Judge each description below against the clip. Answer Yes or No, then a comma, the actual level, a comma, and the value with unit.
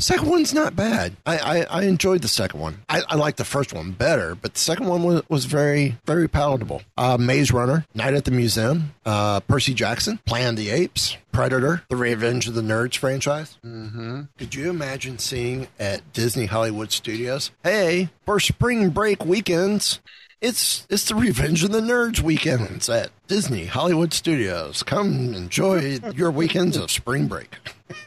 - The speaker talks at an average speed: Yes, average, 170 wpm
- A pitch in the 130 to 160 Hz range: Yes, medium, 140 Hz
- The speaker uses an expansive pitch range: Yes, wide, 6.4 semitones